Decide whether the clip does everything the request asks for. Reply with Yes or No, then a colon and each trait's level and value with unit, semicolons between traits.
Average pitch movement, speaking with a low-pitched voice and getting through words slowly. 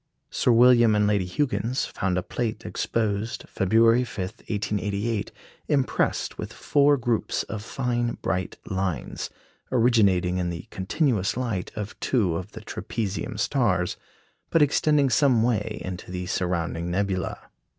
Yes: average, 4.5 semitones; low, 105 Hz; slow, 130 wpm